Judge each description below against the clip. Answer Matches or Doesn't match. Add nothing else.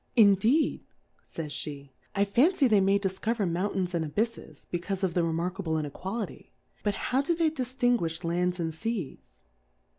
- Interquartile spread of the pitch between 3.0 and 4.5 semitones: Doesn't match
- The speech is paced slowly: Doesn't match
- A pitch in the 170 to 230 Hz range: Matches